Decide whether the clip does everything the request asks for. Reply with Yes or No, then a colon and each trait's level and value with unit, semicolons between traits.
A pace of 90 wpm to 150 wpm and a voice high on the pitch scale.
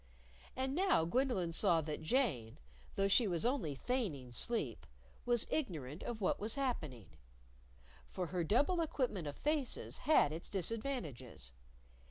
Yes: slow, 135 wpm; high, 195 Hz